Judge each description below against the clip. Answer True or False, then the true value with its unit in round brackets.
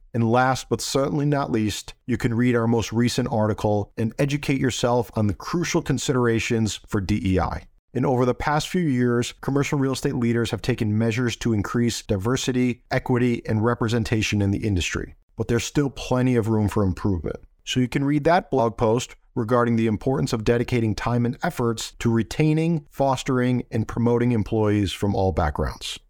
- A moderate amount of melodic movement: True (3.0 semitones)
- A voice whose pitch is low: True (120 Hz)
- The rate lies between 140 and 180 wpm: True (175 wpm)